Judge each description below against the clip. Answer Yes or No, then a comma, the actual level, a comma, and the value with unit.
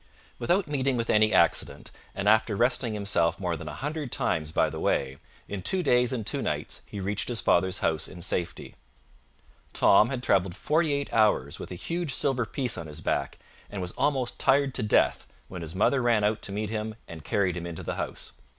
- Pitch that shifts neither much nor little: No, wide, 6.2 semitones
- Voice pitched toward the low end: Yes, low, 105 Hz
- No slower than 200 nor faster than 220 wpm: Yes, fast, 205 wpm